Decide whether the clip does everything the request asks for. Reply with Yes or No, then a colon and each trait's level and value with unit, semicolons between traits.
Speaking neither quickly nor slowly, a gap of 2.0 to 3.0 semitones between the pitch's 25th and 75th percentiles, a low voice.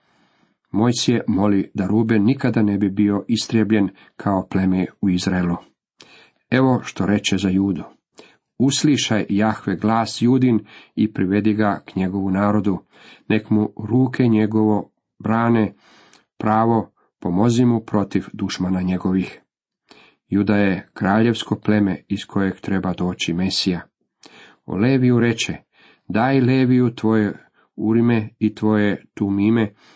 Yes: average, 120 wpm; average, 2.7 semitones; low, 105 Hz